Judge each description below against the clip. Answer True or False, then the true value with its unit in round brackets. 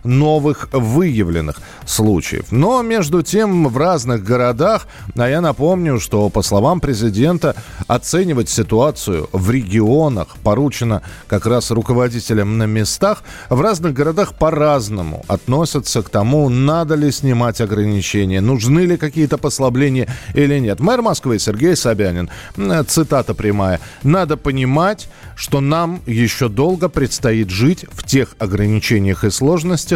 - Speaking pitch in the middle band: False (125 Hz)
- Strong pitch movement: True (6.1 semitones)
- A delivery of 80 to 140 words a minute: True (125 wpm)